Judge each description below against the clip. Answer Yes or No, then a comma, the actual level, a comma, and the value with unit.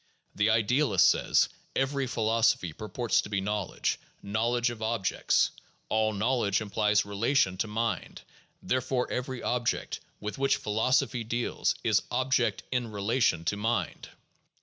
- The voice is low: Yes, low, 115 Hz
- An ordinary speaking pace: No, slow, 130 wpm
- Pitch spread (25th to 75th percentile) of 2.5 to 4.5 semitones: Yes, average, 3.0 semitones